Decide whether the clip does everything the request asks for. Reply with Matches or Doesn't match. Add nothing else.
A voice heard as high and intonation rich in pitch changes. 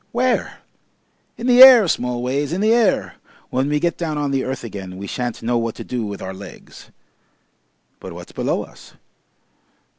Doesn't match